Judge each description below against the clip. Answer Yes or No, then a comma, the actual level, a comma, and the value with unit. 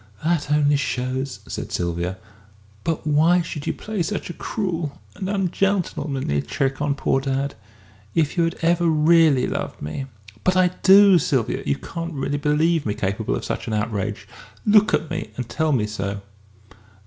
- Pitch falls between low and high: Yes, medium, 150 Hz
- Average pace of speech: Yes, average, 170 wpm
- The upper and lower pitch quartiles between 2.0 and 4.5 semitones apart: No, average, 5.0 semitones